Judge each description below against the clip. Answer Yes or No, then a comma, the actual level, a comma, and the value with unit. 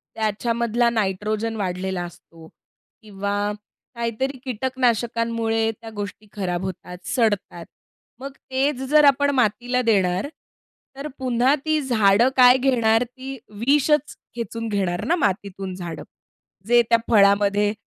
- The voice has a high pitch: Yes, high, 225 Hz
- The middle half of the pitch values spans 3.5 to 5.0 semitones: Yes, average, 4.0 semitones